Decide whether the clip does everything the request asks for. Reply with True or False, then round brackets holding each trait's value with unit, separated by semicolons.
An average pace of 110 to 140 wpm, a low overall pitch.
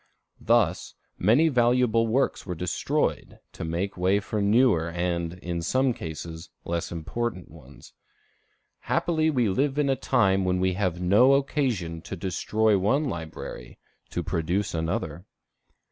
True (135 wpm; 95 Hz)